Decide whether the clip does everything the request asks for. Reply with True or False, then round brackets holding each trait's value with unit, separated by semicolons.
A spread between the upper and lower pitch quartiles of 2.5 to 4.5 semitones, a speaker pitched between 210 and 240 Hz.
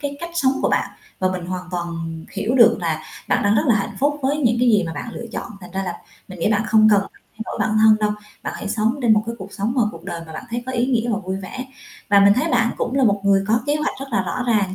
True (4.1 semitones; 215 Hz)